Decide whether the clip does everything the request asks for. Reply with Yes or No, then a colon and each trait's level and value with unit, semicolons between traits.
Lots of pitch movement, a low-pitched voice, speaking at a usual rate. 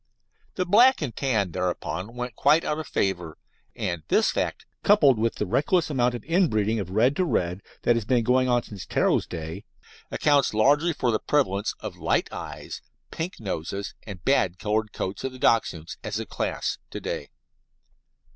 Yes: wide, 6.3 semitones; low, 115 Hz; average, 175 wpm